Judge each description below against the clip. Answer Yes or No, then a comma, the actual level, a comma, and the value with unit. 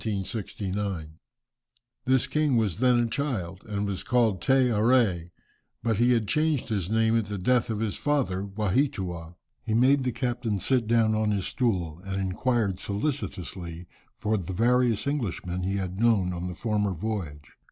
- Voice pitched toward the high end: No, low, 110 Hz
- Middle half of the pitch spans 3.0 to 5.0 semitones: Yes, average, 4.6 semitones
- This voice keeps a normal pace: Yes, average, 160 wpm